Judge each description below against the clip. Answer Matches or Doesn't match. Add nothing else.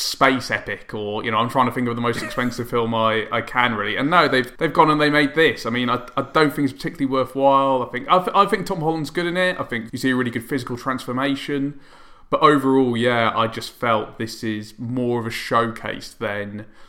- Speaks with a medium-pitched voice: Doesn't match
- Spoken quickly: Matches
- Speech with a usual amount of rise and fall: Matches